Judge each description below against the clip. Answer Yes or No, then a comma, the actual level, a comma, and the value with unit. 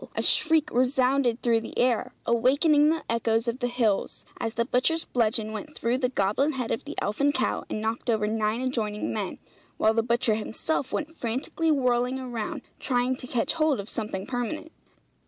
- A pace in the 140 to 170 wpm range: No, average, 180 wpm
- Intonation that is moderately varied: Yes, average, 3.3 semitones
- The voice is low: No, high, 245 Hz